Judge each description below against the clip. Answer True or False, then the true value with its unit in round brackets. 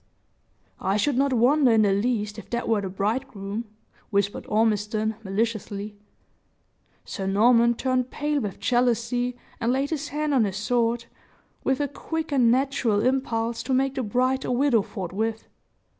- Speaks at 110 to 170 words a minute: True (155 wpm)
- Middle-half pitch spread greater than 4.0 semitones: False (3.7 semitones)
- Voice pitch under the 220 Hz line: False (235 Hz)